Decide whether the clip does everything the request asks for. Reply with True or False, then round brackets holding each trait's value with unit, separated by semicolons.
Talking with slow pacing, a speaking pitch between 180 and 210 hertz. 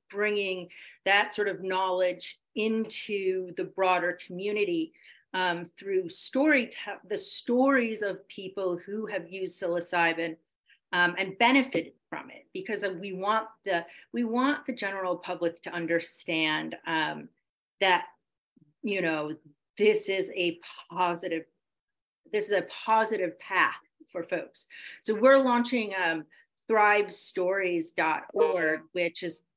True (120 wpm; 190 Hz)